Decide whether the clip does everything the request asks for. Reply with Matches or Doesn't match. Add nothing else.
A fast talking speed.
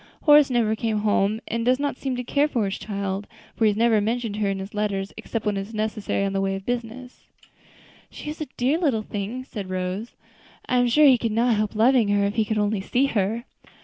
Matches